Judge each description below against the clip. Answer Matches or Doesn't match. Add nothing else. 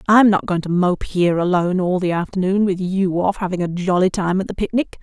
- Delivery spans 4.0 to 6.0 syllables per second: Matches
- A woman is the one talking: Matches